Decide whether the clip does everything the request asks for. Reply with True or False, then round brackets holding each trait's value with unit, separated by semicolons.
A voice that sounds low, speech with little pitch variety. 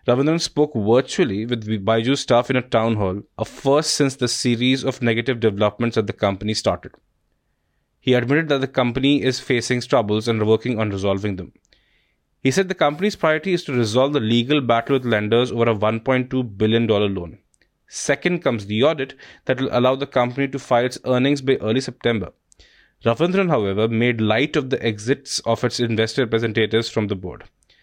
False (120 Hz; 3.6 semitones)